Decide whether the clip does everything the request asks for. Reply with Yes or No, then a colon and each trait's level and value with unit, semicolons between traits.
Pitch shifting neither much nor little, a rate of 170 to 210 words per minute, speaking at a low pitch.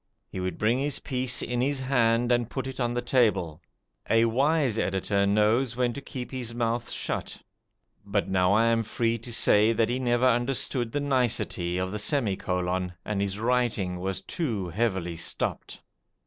Yes: average, 4.0 semitones; average, 175 wpm; low, 115 Hz